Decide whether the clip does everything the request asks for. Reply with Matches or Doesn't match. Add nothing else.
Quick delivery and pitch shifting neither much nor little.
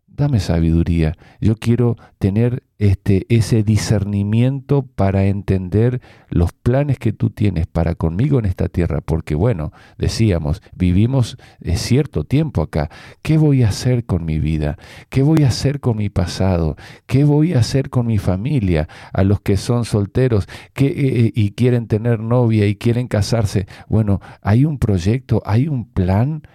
Doesn't match